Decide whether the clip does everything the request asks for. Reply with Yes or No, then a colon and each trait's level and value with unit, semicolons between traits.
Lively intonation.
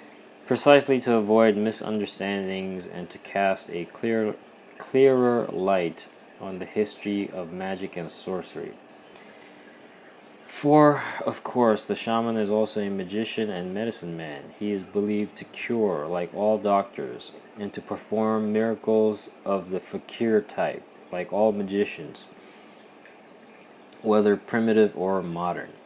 No: narrow, 2.5 semitones